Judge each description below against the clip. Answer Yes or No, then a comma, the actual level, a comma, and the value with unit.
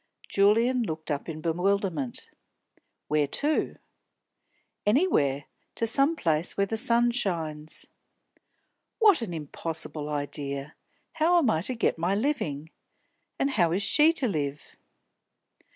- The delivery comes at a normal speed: No, slow, 120 wpm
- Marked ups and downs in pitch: Yes, wide, 7.9 semitones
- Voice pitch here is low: No, medium, 180 Hz